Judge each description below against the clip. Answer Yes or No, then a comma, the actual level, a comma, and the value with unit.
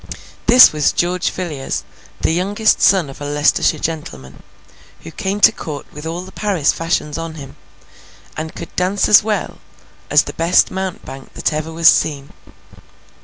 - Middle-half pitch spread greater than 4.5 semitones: No, average, 4.0 semitones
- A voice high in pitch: No, medium, 165 Hz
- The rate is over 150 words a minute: Yes, average, 160 wpm